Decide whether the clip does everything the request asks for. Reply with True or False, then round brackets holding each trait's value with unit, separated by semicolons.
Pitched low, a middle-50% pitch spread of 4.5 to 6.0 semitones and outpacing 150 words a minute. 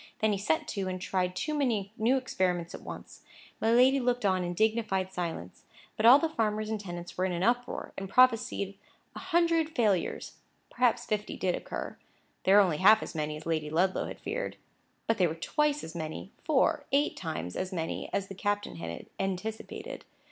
False (200 Hz; 5.2 semitones; 190 wpm)